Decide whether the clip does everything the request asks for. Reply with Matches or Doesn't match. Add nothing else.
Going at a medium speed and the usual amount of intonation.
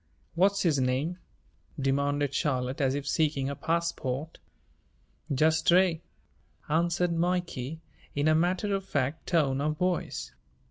Doesn't match